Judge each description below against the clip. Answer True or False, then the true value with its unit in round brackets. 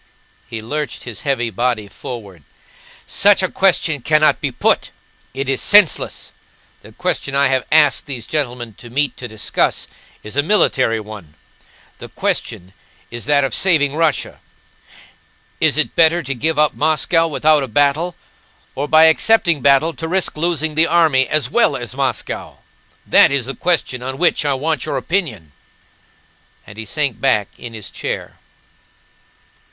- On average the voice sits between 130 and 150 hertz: True (140 Hz)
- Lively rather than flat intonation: False (4.7 semitones)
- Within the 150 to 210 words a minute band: True (155 wpm)